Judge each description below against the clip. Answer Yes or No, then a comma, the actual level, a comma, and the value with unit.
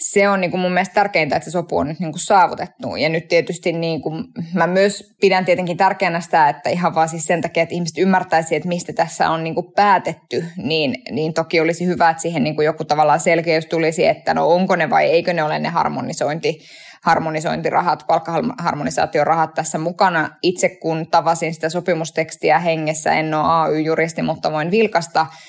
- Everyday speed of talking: No, fast, 180 wpm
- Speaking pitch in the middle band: Yes, medium, 165 Hz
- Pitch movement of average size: No, narrow, 1.9 semitones